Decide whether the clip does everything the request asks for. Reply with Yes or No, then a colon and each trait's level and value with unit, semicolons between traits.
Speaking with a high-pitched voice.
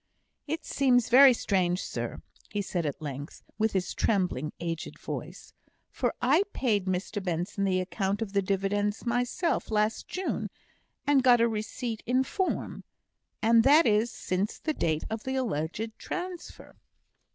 Yes: high, 215 Hz